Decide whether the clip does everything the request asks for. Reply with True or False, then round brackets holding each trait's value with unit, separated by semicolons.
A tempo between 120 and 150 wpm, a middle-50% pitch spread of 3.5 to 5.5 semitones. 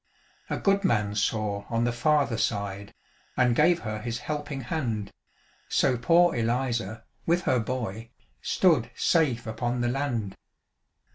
True (135 wpm; 4.6 semitones)